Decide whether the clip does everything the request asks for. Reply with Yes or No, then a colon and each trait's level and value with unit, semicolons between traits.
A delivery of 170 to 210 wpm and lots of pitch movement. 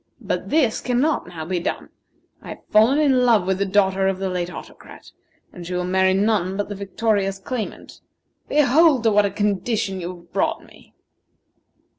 No: average, 180 wpm; average, 3.4 semitones